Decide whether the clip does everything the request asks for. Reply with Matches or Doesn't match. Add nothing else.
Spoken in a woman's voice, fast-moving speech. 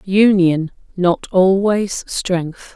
Doesn't match